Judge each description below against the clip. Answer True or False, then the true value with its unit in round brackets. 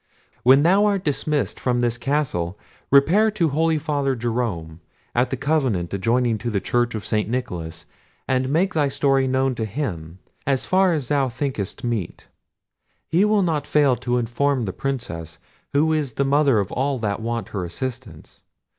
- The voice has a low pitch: True (130 Hz)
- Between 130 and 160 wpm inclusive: False (170 wpm)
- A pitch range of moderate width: True (4.5 semitones)